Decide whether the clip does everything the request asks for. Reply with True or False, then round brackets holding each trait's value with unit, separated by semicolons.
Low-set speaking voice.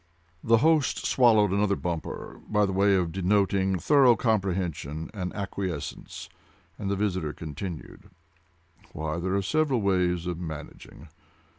True (95 Hz)